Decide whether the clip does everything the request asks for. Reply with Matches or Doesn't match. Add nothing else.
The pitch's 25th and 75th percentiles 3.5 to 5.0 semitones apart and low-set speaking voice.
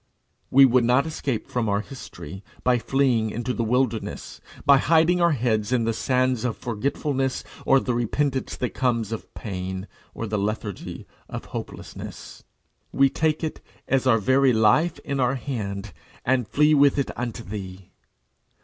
Matches